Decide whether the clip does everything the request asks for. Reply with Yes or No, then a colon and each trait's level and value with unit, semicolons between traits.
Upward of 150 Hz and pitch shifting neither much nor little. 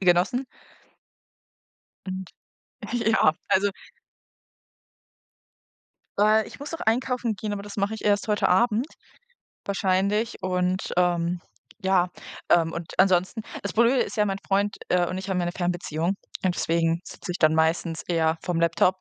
Yes: medium, 185 Hz; average, 3.1 semitones